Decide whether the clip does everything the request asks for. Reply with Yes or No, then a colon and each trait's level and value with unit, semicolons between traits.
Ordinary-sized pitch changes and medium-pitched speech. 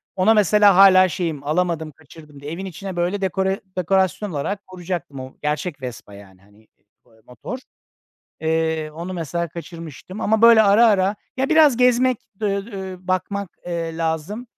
Yes: average, 4.1 semitones; medium, 180 Hz